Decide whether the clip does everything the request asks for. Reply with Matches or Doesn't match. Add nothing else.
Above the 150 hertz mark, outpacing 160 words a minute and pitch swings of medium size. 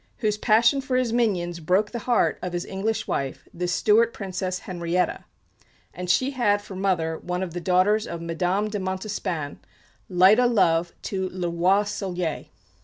Matches